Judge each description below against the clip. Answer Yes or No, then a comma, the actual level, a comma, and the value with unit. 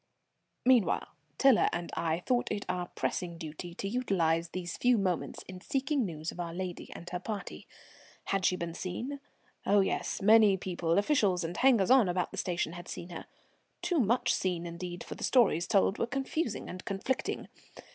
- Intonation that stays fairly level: No, average, 5.0 semitones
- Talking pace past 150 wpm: Yes, average, 175 wpm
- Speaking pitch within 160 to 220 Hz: Yes, medium, 185 Hz